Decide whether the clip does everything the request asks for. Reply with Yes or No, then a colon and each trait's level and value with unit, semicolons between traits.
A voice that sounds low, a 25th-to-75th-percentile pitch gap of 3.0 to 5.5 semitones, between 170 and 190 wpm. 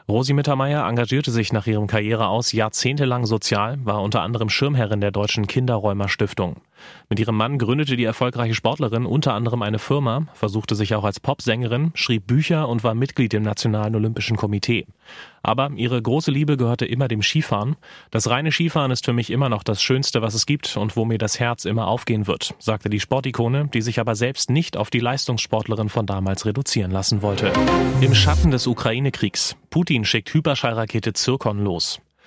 Yes: low, 115 Hz; average, 3.3 semitones; average, 180 wpm